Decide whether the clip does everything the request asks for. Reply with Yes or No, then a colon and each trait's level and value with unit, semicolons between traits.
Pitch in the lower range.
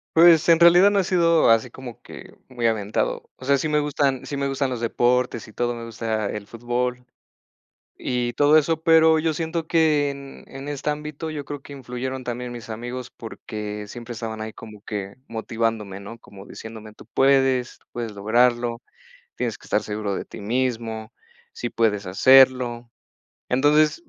Yes: low, 125 Hz